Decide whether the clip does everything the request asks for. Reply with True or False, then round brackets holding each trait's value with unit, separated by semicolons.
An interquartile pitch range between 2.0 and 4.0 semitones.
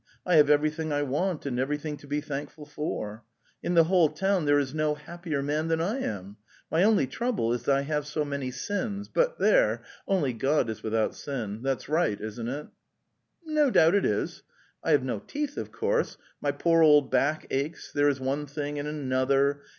True (3.5 semitones)